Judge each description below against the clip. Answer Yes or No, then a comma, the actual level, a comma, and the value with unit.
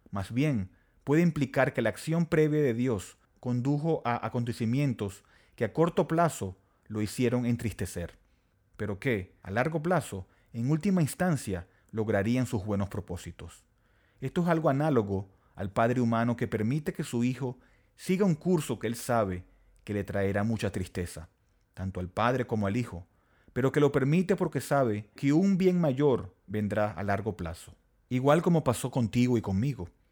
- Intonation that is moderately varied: No, wide, 5.9 semitones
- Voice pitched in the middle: No, low, 115 Hz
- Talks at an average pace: Yes, average, 160 wpm